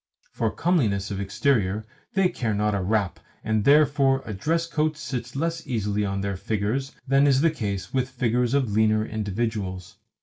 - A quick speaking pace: No, average, 170 wpm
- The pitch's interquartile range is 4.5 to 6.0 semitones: Yes, average, 5.2 semitones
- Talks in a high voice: No, low, 110 Hz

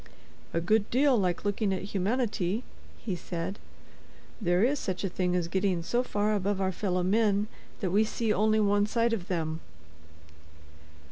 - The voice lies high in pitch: Yes, high, 200 Hz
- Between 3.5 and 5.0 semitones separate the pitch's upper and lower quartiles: No, average, 3.1 semitones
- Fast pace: No, average, 160 wpm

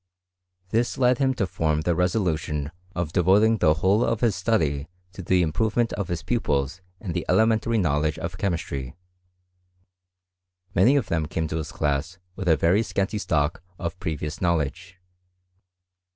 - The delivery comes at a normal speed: Yes, average, 150 wpm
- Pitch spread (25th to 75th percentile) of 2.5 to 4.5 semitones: No, average, 5.1 semitones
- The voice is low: Yes, very low, 90 Hz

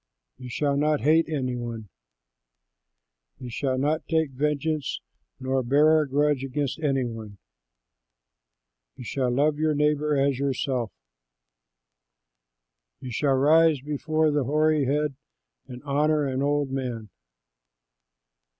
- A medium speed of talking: No, slow, 120 wpm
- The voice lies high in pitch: No, medium, 140 Hz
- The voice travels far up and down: No, average, 2.7 semitones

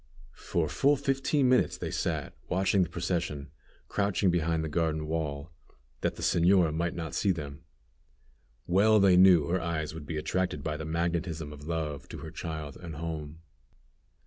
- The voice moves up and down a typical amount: Yes, average, 3.0 semitones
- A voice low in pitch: Yes, very low, 85 Hz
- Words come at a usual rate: Yes, average, 165 wpm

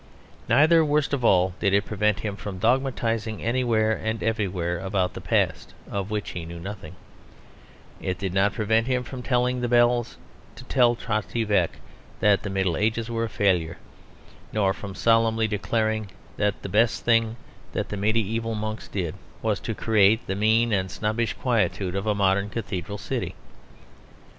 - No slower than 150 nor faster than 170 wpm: Yes, average, 165 wpm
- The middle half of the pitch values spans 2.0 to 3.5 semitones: Yes, average, 2.7 semitones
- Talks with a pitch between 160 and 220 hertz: No, low, 110 Hz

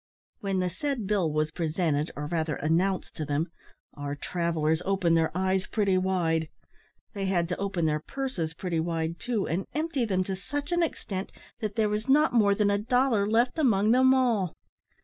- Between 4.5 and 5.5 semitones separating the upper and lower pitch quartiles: Yes, average, 5.1 semitones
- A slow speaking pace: No, average, 185 wpm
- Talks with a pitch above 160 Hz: Yes, high, 190 Hz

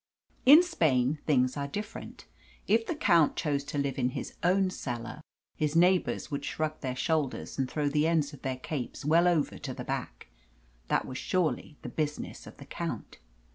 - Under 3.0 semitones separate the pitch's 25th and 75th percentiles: No, average, 4.1 semitones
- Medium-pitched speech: Yes, medium, 150 Hz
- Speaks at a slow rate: No, average, 180 wpm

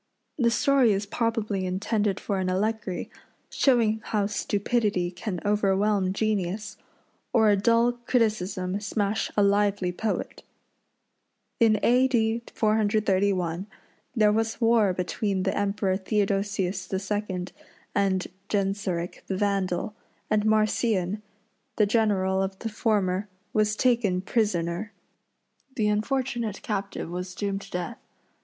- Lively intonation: No, narrow, 2.4 semitones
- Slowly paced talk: Yes, slow, 115 wpm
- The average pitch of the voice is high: Yes, high, 205 Hz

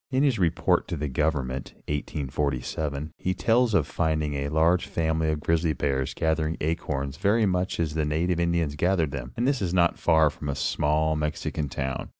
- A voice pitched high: No, very low, 80 Hz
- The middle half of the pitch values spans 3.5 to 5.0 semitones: No, average, 2.9 semitones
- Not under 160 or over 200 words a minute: Yes, average, 175 wpm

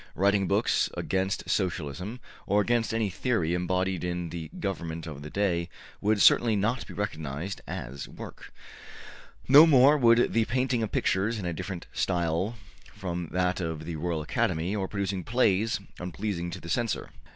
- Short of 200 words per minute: Yes, average, 160 wpm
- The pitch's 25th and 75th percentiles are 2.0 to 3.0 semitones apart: No, average, 4.1 semitones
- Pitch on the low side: Yes, very low, 95 Hz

